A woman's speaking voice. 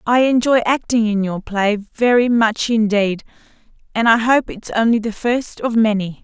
Yes: female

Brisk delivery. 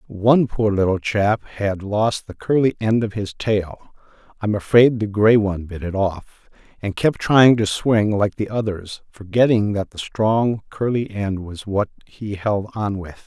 No: average, 170 wpm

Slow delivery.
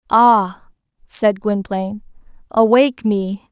Yes: slow, 85 wpm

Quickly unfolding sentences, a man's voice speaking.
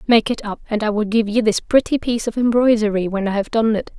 No: fast, 270 wpm; female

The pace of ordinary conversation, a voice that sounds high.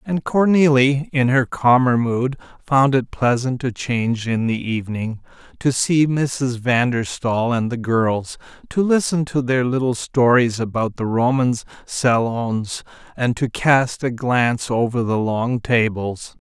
No: average, 155 wpm; low, 125 Hz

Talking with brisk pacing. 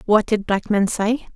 Yes: fast, 220 wpm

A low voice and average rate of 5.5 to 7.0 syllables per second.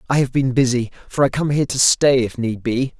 Yes: low, 130 Hz; 5.7 syllables/s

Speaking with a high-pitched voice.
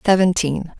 No: medium, 175 Hz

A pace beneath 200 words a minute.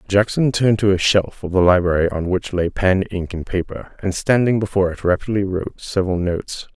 No: fast, 205 wpm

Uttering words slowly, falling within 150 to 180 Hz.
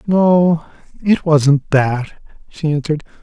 Yes: slow, 95 wpm; medium, 155 Hz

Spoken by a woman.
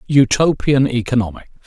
No: male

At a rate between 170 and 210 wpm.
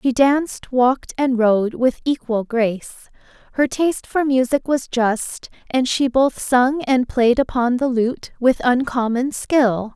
No: average, 155 wpm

